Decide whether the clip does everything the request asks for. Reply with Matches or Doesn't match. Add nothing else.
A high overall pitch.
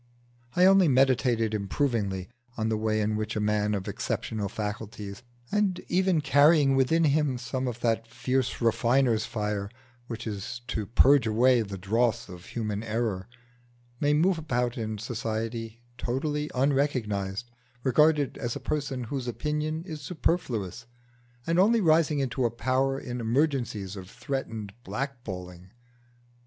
Doesn't match